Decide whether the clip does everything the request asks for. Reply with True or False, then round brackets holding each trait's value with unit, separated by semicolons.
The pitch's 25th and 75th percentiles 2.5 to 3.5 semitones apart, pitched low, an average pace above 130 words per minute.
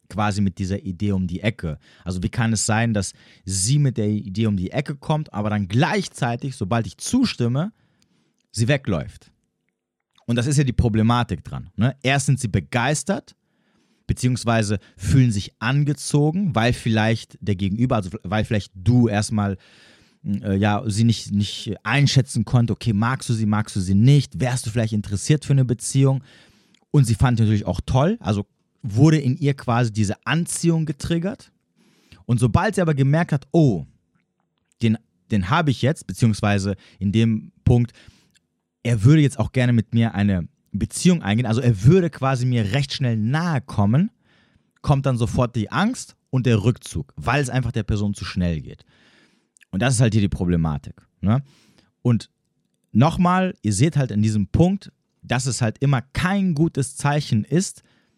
False (4.8 semitones; 120 Hz; 170 wpm)